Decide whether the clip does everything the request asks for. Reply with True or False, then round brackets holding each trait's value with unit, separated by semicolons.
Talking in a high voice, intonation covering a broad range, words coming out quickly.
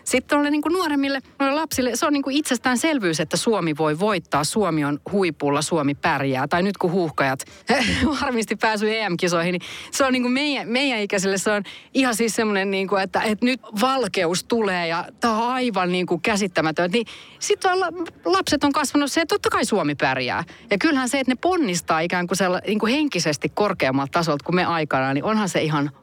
True (215 Hz; 7.5 semitones; 185 wpm)